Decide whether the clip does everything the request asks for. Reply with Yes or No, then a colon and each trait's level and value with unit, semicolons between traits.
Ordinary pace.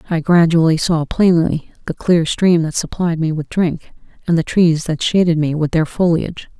Yes: average, 190 wpm